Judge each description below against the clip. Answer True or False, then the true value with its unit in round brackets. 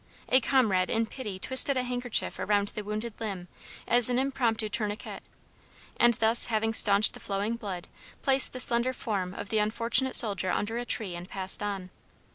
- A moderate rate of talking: True (175 wpm)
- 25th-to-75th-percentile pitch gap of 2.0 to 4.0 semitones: True (3.2 semitones)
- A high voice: True (220 Hz)